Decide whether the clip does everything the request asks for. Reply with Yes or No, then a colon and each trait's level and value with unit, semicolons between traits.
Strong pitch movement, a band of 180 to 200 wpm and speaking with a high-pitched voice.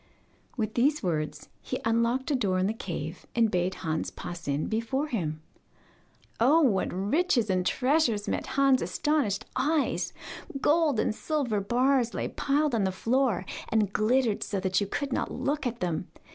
No: wide, 6.1 semitones; average, 165 wpm; high, 230 Hz